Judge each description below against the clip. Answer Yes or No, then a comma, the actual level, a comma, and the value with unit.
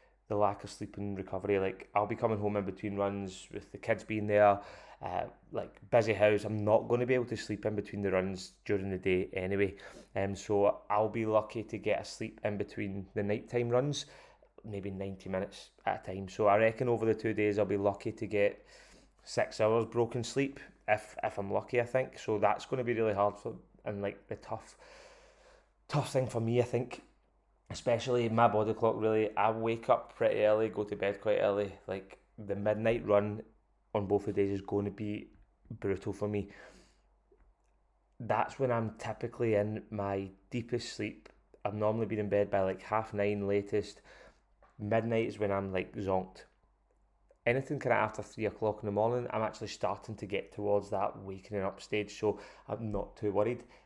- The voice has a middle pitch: No, low, 105 Hz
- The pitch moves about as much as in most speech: No, narrow, 2.0 semitones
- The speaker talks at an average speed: Yes, average, 195 wpm